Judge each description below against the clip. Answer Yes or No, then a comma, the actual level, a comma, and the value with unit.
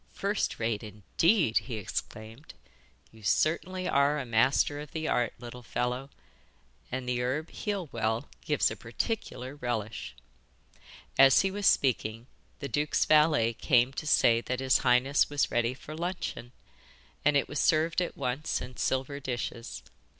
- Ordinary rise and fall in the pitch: Yes, average, 4.3 semitones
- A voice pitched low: Yes, low, 130 Hz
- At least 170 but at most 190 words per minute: No, average, 150 wpm